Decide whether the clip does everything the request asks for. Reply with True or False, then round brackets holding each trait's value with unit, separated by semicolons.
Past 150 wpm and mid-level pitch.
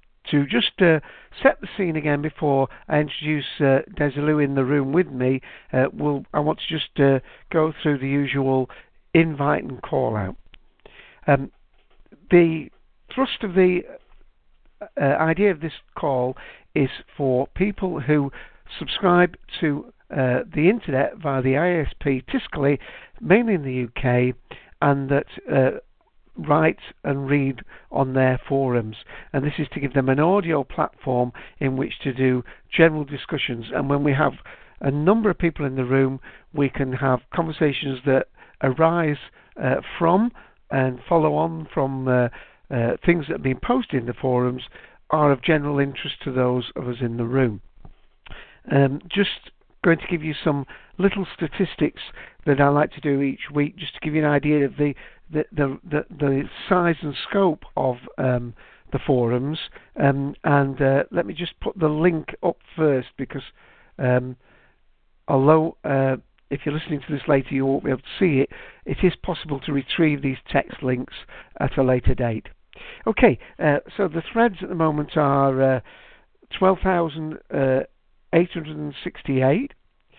True (160 wpm; 145 Hz)